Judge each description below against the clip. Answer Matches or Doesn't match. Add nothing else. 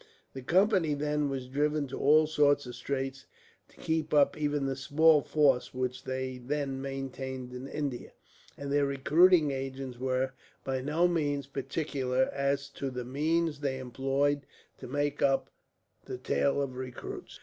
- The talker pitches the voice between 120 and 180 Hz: Matches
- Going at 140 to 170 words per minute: Matches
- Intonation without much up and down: Matches